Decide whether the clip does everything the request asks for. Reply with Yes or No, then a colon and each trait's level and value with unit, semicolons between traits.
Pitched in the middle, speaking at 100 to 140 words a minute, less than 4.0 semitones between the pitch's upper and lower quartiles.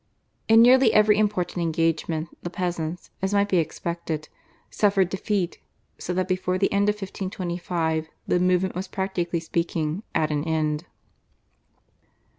Yes: medium, 180 Hz; slow, 135 wpm; average, 2.9 semitones